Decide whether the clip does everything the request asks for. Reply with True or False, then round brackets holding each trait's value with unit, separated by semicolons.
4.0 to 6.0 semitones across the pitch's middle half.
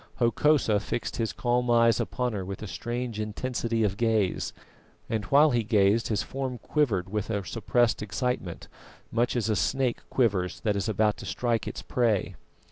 False (2.9 semitones)